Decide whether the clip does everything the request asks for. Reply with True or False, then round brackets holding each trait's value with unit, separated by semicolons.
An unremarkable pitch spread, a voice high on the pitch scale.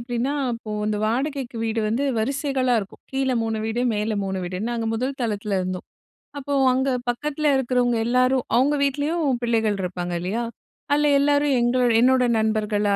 True (3.8 semitones; 240 Hz)